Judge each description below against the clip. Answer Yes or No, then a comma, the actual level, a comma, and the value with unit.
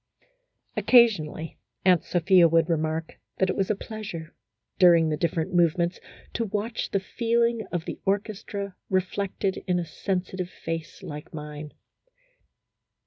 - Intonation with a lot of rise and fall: No, average, 3.4 semitones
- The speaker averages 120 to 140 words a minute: Yes, slow, 135 wpm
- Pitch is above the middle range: No, medium, 180 Hz